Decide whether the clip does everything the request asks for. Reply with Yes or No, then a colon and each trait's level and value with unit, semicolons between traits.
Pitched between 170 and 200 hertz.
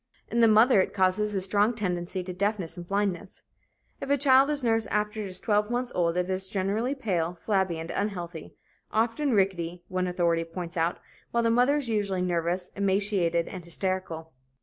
Yes: high, 190 Hz